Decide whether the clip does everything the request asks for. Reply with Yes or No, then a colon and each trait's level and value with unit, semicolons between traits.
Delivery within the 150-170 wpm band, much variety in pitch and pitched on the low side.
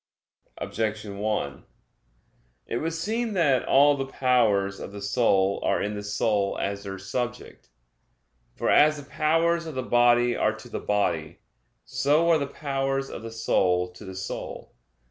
Yes: average, 160 wpm; wide, 5.9 semitones; low, 120 Hz